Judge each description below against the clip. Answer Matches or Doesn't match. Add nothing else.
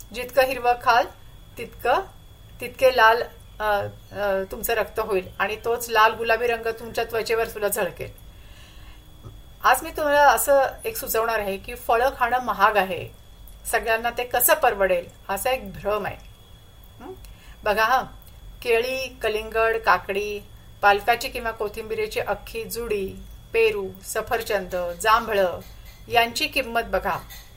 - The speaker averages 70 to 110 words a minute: Doesn't match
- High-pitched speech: Matches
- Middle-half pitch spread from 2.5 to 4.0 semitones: Matches